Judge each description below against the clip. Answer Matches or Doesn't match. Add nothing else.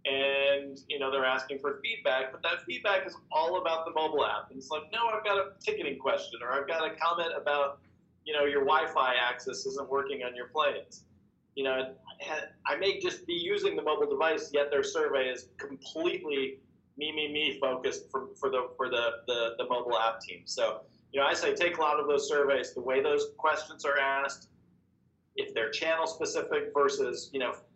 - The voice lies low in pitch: Doesn't match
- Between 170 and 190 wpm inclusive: Doesn't match